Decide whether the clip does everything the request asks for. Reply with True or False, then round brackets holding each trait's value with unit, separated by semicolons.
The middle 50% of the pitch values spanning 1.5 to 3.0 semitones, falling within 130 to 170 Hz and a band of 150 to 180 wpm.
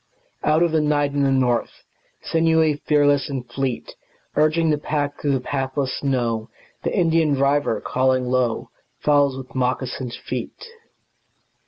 False (2.7 semitones; 140 Hz; 140 wpm)